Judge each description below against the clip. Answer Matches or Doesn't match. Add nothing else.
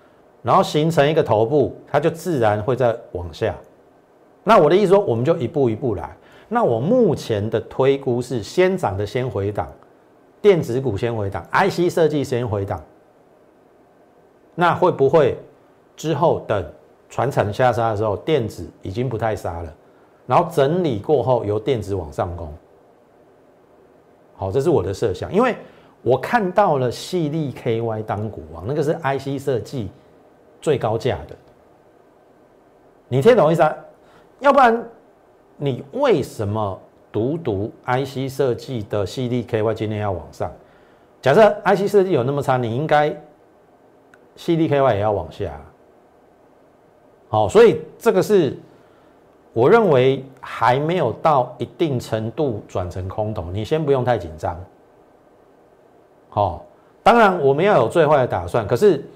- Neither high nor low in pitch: Doesn't match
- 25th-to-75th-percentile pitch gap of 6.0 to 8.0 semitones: Matches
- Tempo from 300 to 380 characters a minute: Doesn't match